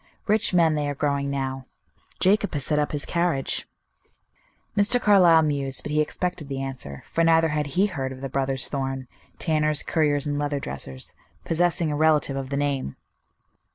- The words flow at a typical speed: Yes, average, 175 wpm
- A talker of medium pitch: Yes, medium, 145 Hz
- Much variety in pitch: No, average, 3.3 semitones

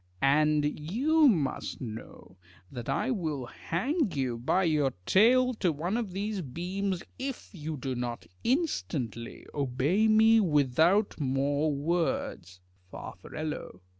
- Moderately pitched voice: Yes, medium, 160 Hz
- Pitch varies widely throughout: Yes, wide, 7.5 semitones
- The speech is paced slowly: Yes, slow, 120 wpm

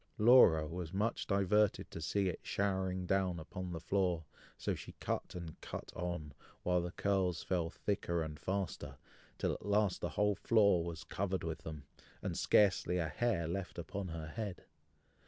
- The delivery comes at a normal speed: Yes, average, 170 wpm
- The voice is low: Yes, very low, 90 Hz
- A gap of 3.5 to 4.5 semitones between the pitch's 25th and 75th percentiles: No, average, 3.0 semitones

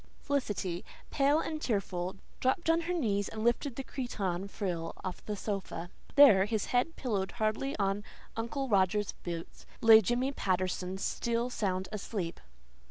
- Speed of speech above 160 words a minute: No, average, 145 wpm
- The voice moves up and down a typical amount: Yes, average, 5.0 semitones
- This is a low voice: No, high, 210 Hz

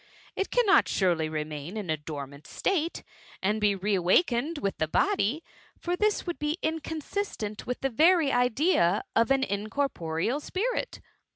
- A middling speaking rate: Yes, average, 150 wpm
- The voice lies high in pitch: Yes, high, 240 Hz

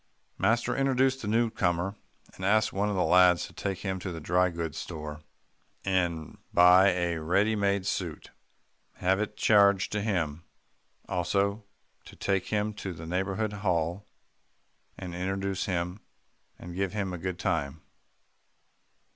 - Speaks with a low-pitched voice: Yes, very low, 95 Hz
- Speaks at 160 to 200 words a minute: No, average, 145 wpm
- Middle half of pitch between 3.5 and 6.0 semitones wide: No, average, 2.7 semitones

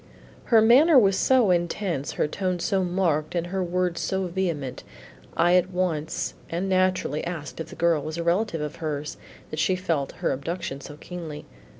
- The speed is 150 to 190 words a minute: Yes, average, 180 wpm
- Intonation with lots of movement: No, average, 3.3 semitones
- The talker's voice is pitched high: No, medium, 175 Hz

